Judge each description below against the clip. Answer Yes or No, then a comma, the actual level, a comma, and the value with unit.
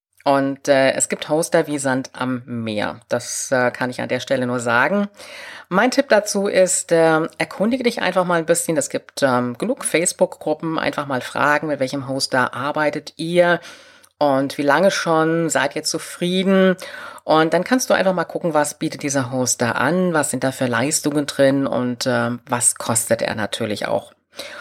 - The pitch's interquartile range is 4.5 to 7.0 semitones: Yes, average, 4.8 semitones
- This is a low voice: No, medium, 150 Hz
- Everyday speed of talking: Yes, average, 180 wpm